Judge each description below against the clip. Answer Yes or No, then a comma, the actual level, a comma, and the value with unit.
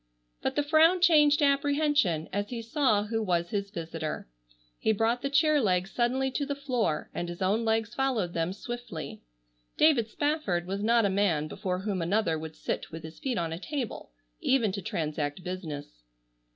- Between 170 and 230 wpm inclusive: Yes, average, 180 wpm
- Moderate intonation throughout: No, wide, 7.7 semitones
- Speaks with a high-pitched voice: Yes, high, 215 Hz